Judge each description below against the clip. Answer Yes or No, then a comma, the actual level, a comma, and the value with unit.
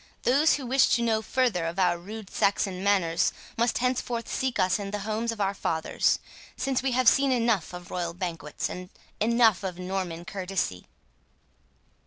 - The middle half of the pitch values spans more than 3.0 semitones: Yes, average, 4.7 semitones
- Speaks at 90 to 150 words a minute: No, average, 170 wpm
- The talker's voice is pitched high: Yes, high, 200 Hz